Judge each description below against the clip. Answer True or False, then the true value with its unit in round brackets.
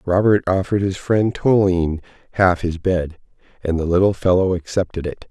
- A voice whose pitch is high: False (90 Hz)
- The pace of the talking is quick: False (160 wpm)